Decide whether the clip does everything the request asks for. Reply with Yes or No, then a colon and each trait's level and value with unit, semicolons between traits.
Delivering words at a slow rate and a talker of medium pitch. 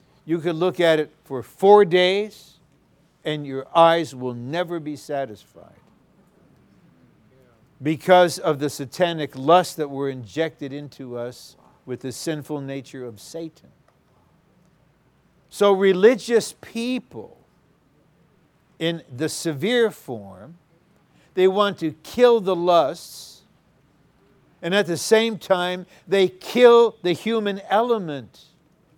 Yes: slow, 110 wpm; medium, 165 Hz